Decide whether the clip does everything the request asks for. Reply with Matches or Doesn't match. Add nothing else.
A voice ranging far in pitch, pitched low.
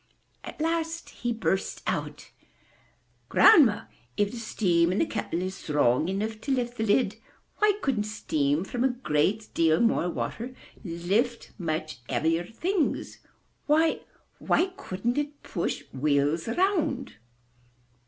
Doesn't match